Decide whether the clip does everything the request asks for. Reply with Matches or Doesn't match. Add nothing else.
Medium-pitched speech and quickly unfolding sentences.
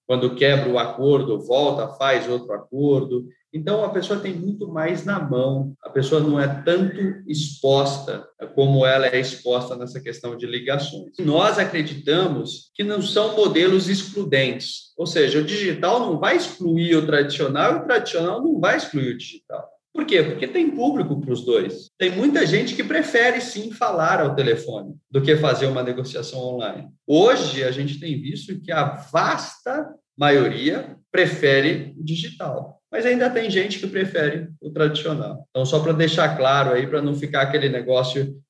Doesn't match